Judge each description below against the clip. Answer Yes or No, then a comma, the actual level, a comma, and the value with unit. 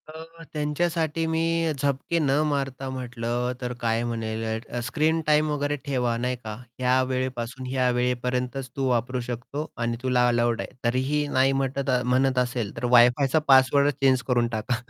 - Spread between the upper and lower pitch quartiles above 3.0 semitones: No, average, 2.7 semitones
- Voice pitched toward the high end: No, low, 130 Hz